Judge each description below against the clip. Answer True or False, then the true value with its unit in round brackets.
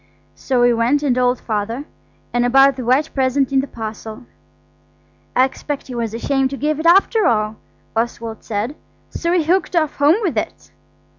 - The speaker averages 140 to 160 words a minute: False (175 wpm)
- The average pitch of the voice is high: True (260 Hz)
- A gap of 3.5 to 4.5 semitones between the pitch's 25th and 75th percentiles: True (3.9 semitones)